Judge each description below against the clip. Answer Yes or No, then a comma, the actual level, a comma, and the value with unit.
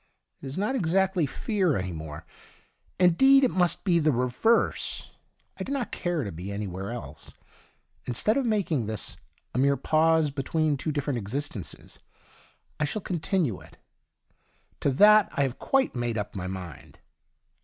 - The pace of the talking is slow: No, average, 160 wpm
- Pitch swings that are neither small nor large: No, wide, 9.0 semitones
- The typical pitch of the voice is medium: Yes, medium, 145 Hz